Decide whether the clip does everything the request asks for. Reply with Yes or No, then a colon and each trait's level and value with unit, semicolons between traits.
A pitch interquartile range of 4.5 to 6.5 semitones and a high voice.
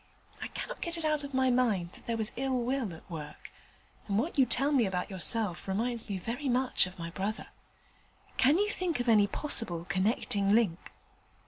Yes: wide, 5.6 semitones; high, 230 Hz